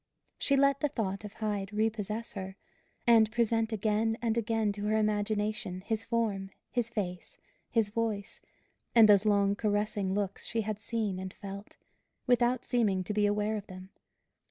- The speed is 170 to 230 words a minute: No, average, 160 wpm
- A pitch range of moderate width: No, narrow, 2.0 semitones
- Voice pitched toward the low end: No, high, 215 Hz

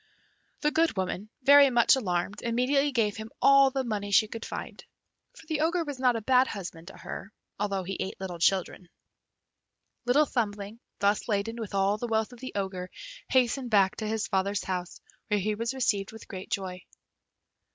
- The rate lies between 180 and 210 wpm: Yes, average, 185 wpm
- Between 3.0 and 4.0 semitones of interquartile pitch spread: No, average, 4.5 semitones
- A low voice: No, high, 215 Hz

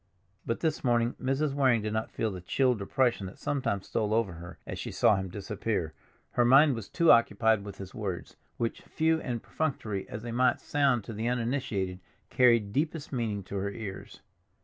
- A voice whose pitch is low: Yes, low, 115 Hz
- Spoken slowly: No, average, 190 wpm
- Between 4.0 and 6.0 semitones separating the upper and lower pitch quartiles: Yes, average, 4.3 semitones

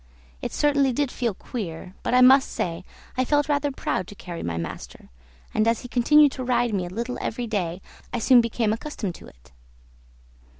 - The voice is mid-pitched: No, high, 235 Hz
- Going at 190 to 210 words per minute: Yes, average, 195 wpm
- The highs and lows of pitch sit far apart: Yes, wide, 5.7 semitones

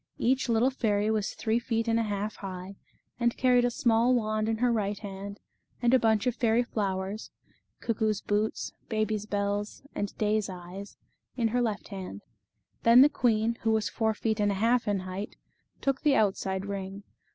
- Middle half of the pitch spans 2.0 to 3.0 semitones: Yes, narrow, 2.5 semitones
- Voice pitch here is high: Yes, high, 215 Hz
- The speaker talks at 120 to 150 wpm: No, average, 180 wpm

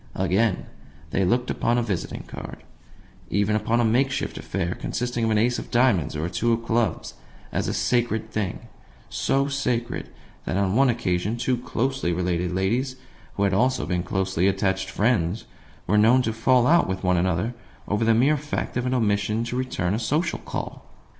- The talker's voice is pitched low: Yes, low, 110 Hz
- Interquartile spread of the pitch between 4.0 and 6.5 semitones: Yes, average, 4.5 semitones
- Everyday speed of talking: Yes, average, 185 wpm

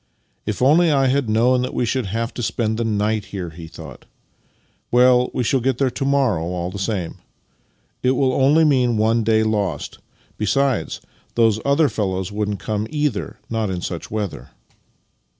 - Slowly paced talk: No, average, 185 wpm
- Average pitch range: Yes, average, 4.1 semitones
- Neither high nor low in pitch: No, low, 115 Hz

